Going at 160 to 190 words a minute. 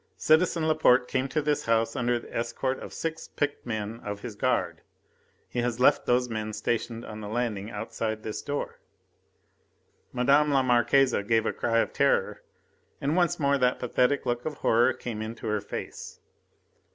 Yes: average, 170 wpm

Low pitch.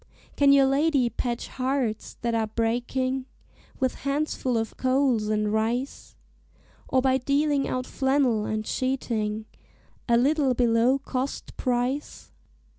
No: very high, 255 Hz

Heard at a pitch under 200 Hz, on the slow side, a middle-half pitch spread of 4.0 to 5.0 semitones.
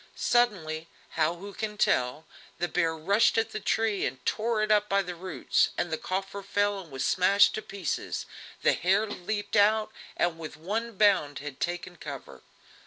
No: high, 190 Hz; average, 175 wpm; average, 4.4 semitones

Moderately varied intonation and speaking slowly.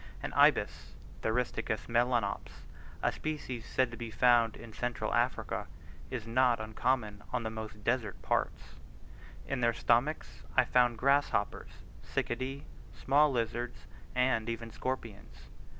No: narrow, 2.3 semitones; slow, 125 wpm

